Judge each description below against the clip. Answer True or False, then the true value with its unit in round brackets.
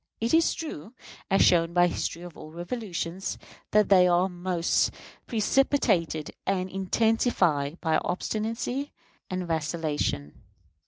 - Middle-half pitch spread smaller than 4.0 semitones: False (4.5 semitones)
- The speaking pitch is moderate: True (180 Hz)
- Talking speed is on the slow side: True (120 wpm)